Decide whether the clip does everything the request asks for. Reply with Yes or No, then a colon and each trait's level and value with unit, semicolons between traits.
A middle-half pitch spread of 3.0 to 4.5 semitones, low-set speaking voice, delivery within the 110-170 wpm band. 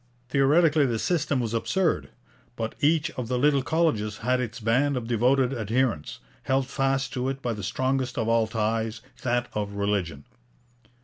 Yes: average, 3.3 semitones; low, 125 Hz; average, 165 wpm